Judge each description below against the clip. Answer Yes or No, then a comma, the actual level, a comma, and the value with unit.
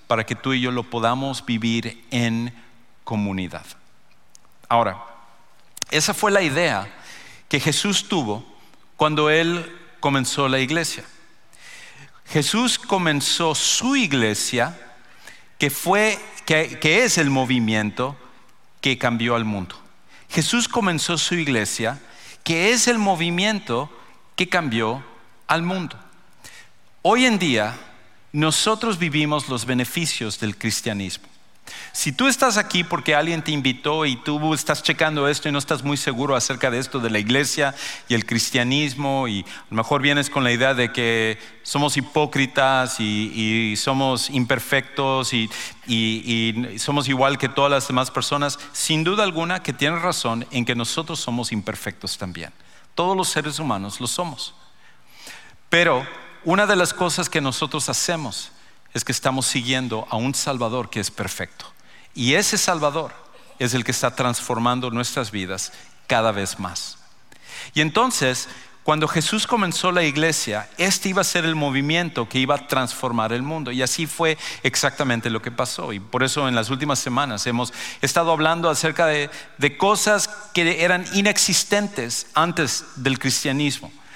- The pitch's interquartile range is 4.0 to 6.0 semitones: Yes, average, 5.3 semitones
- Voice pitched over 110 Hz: Yes, low, 135 Hz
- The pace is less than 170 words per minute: Yes, average, 150 wpm